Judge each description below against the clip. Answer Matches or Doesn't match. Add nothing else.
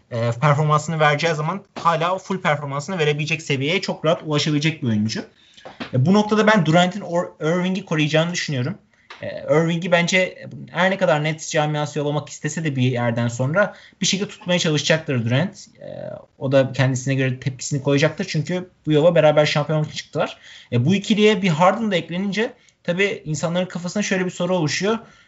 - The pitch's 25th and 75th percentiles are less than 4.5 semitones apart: Matches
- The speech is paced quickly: Matches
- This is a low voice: Doesn't match